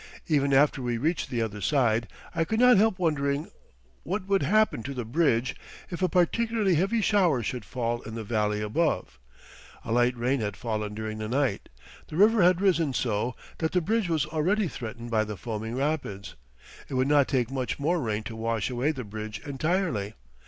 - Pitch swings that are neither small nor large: No, wide, 7.0 semitones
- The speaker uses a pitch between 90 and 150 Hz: Yes, low, 135 Hz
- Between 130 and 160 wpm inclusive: No, average, 190 wpm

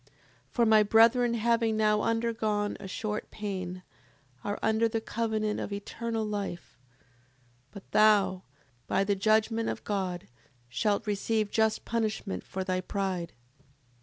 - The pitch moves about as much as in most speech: No, narrow, 2.1 semitones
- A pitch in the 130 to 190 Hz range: No, high, 215 Hz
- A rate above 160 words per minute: No, slow, 135 wpm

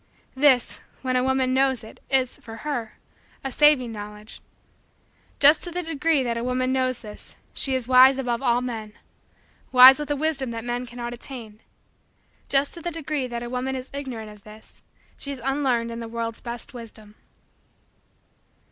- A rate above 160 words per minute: Yes, average, 175 wpm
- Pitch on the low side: No, very high, 255 Hz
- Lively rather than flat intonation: No, narrow, 2.6 semitones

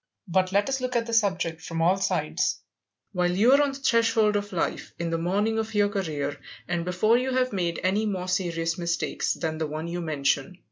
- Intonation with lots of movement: No, average, 4.7 semitones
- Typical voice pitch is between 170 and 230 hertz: Yes, medium, 185 Hz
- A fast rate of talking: Yes, fast, 215 wpm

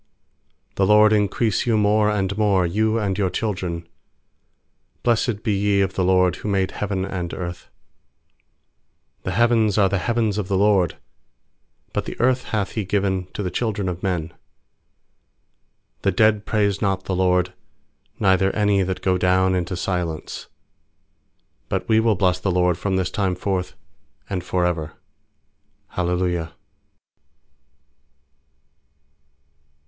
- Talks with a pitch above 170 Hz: No, very low, 95 Hz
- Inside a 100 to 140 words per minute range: Yes, slow, 135 wpm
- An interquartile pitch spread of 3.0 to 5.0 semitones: No, narrow, 2.5 semitones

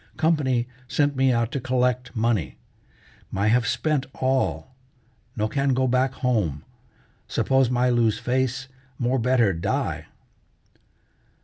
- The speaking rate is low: Yes, slow, 120 wpm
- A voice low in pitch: Yes, low, 125 Hz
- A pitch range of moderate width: No, narrow, 2.1 semitones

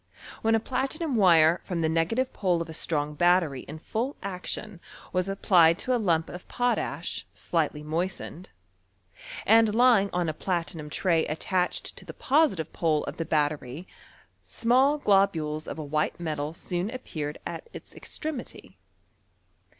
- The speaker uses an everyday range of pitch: No, wide, 5.7 semitones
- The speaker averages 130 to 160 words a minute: Yes, average, 150 wpm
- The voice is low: No, medium, 175 Hz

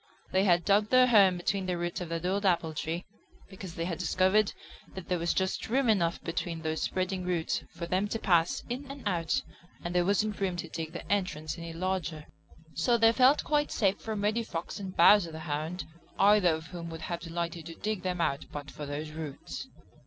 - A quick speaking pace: Yes, fast, 210 wpm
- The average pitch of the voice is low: No, medium, 180 Hz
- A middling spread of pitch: Yes, average, 3.3 semitones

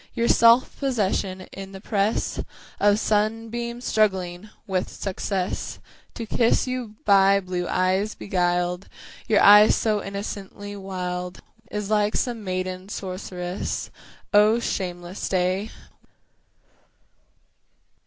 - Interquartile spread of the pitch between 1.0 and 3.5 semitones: Yes, average, 2.7 semitones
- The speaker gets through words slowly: Yes, slow, 105 wpm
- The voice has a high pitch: Yes, high, 200 Hz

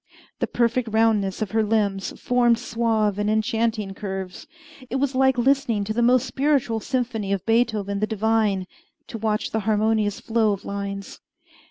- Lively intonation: No, narrow, 2.4 semitones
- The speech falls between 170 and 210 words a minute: No, average, 160 wpm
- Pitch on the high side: Yes, high, 220 Hz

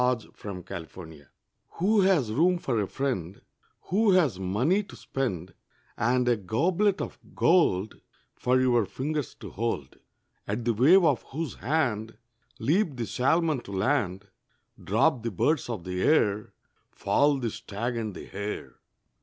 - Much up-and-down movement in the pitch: Yes, wide, 7.2 semitones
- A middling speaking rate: Yes, average, 150 wpm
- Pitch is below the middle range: Yes, low, 120 Hz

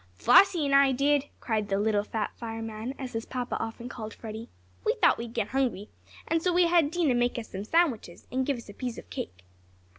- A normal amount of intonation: Yes, average, 4.0 semitones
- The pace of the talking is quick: Yes, fast, 210 wpm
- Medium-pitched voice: No, high, 240 Hz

